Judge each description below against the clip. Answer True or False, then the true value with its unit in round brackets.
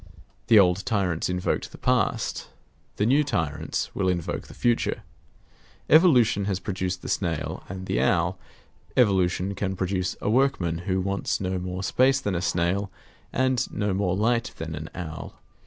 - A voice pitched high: False (95 Hz)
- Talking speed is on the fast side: False (155 wpm)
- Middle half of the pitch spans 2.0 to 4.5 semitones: True (3.2 semitones)